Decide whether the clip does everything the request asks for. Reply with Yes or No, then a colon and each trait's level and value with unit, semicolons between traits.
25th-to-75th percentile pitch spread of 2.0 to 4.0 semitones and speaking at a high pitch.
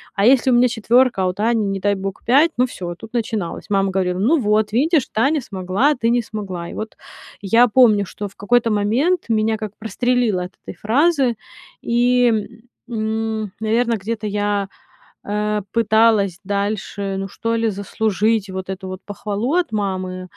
Yes: average, 3.1 semitones; high, 215 Hz